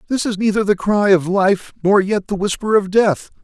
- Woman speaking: No, male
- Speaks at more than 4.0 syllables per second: Yes, 5.0 syllables/s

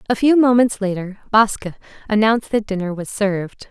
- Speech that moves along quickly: No, average, 160 wpm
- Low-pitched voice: No, high, 210 Hz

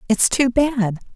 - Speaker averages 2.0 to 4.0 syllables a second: Yes, 3.4 syllables/s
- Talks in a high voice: Yes, high, 240 Hz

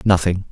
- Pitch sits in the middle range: No, very low, 90 Hz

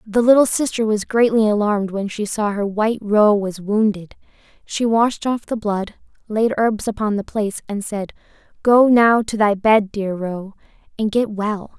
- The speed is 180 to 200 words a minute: Yes, average, 185 wpm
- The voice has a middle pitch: No, high, 210 Hz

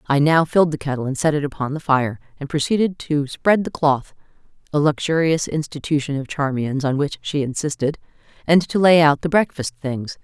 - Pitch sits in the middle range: Yes, medium, 150 Hz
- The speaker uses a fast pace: No, average, 195 wpm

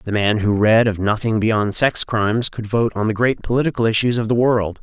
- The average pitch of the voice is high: No, low, 110 Hz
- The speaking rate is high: Yes, fast, 235 wpm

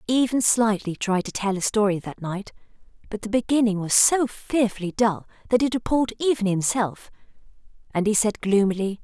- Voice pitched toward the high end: Yes, high, 215 Hz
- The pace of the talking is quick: No, average, 165 wpm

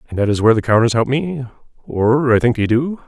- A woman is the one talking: No, male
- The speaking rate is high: Yes, fast, 235 wpm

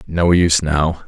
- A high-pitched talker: No, very low, 80 Hz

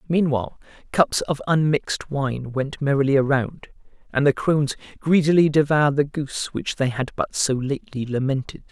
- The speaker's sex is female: No, male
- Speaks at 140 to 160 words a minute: Yes, average, 150 wpm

